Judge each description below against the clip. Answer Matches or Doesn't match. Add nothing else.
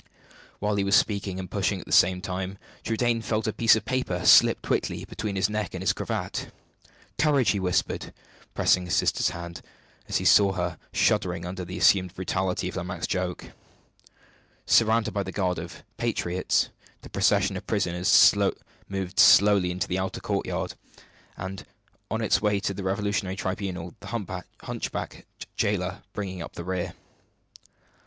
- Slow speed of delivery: Doesn't match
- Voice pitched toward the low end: Matches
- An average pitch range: Doesn't match